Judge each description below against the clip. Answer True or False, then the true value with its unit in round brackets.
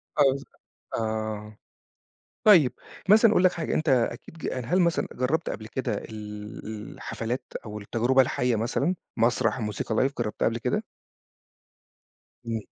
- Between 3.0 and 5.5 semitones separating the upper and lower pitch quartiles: True (4.1 semitones)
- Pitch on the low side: True (120 Hz)